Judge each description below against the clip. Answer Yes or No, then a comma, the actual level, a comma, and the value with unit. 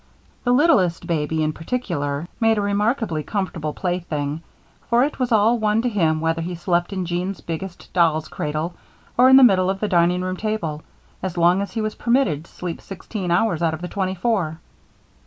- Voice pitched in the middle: Yes, medium, 180 Hz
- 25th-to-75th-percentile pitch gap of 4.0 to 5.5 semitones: Yes, average, 4.7 semitones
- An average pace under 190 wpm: No, average, 195 wpm